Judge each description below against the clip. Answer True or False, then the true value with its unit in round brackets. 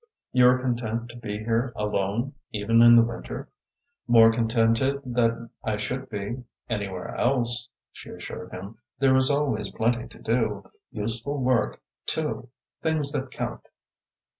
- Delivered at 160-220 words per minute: False (140 wpm)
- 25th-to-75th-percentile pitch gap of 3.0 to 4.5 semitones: False (2.5 semitones)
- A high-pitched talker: False (115 Hz)